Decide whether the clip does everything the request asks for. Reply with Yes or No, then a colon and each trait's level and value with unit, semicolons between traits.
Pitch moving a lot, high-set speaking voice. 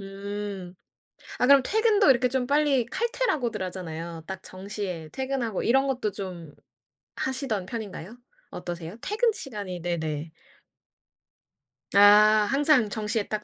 Yes: wide, 6.4 semitones; high, 210 Hz